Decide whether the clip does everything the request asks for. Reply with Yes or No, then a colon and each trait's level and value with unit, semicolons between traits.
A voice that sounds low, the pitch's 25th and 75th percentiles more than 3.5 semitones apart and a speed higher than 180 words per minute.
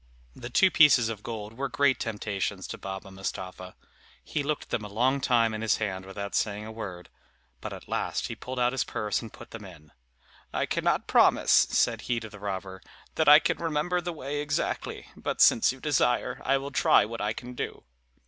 Yes: low, 115 Hz; average, 5.1 semitones; fast, 205 wpm